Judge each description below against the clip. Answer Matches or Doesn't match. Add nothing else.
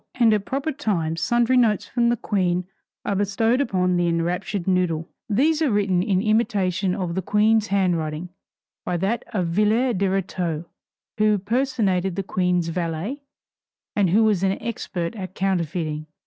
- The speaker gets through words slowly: Doesn't match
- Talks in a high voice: Matches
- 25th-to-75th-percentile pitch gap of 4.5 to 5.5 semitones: Doesn't match